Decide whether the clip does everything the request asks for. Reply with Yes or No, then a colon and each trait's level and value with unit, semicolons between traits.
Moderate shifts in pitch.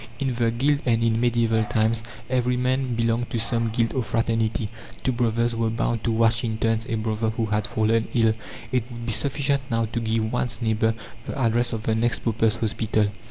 No: narrow, 1.4 semitones